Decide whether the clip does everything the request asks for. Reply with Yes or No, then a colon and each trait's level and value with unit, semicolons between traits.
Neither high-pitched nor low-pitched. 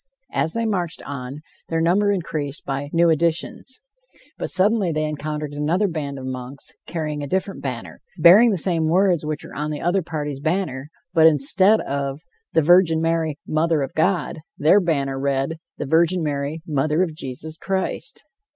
Yes: medium, 160 Hz